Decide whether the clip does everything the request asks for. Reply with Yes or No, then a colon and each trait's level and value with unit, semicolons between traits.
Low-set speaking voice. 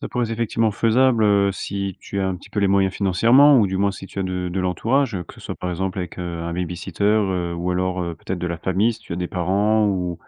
Yes: very low, 95 Hz